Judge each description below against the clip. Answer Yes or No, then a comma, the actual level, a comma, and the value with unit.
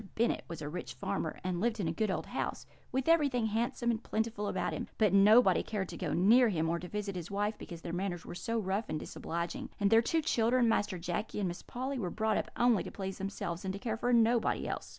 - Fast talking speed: Yes, fast, 245 wpm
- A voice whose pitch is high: Yes, high, 205 Hz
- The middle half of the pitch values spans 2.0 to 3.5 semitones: No, average, 4.3 semitones